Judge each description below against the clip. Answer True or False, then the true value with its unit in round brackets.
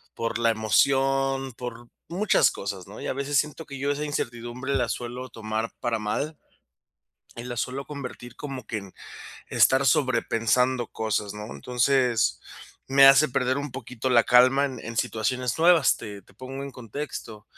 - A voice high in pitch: False (125 Hz)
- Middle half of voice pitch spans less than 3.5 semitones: True (3.1 semitones)